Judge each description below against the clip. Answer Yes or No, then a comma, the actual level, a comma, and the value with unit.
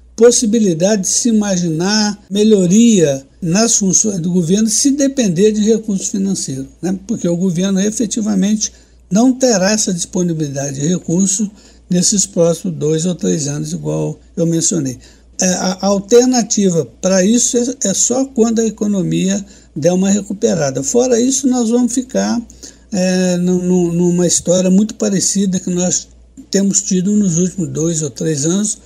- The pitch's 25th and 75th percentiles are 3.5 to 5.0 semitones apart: Yes, average, 3.8 semitones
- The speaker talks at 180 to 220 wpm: No, average, 135 wpm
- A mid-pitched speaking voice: No, high, 195 Hz